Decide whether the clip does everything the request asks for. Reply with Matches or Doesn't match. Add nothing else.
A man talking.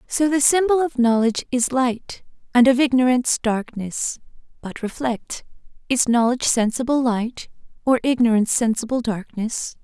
Doesn't match